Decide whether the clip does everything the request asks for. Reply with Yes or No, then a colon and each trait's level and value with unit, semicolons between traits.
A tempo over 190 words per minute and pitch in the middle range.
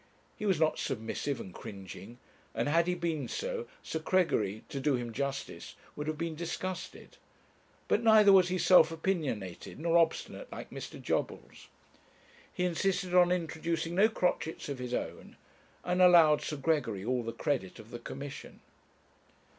No: average, 155 wpm; medium, 160 Hz